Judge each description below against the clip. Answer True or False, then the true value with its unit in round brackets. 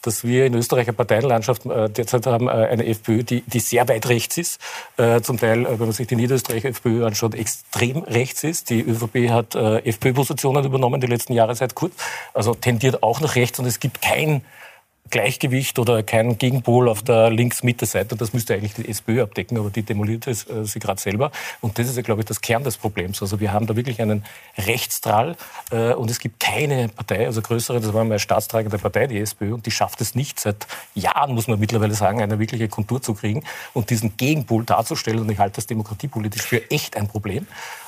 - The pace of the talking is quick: True (205 wpm)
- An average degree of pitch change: False (2.0 semitones)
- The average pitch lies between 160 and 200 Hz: False (115 Hz)